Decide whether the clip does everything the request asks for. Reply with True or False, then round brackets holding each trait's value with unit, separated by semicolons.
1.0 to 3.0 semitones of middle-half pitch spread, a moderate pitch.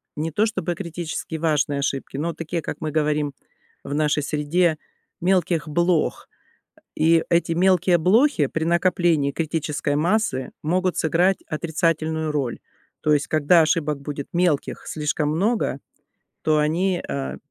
True (2.6 semitones; 160 Hz)